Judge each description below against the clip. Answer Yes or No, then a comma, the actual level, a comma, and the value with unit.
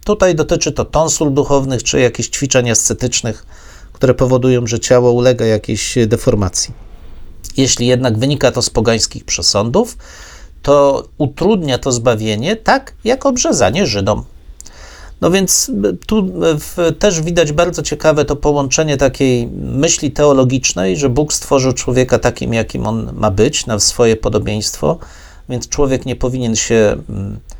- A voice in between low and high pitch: No, low, 130 Hz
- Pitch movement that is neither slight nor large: Yes, average, 4.7 semitones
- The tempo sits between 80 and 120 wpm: No, average, 130 wpm